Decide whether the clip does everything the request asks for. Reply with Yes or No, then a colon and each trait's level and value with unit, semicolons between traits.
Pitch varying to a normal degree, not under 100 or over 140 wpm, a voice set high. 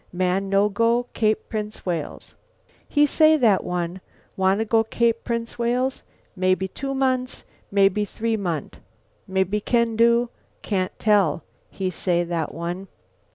Yes: average, 4.0 semitones; slow, 135 wpm; high, 210 Hz